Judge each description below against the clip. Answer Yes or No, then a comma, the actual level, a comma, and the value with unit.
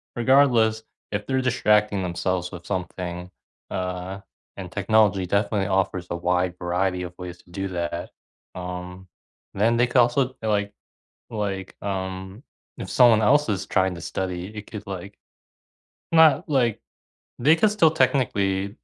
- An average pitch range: Yes, average, 3.4 semitones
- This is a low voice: Yes, very low, 95 Hz